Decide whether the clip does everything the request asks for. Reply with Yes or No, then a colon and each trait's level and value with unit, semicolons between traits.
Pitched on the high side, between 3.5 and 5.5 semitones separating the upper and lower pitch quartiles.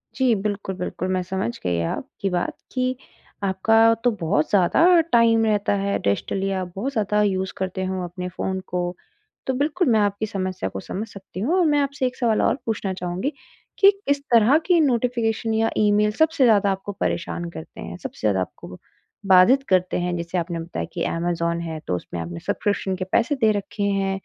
Yes: high, 195 Hz; average, 4.2 semitones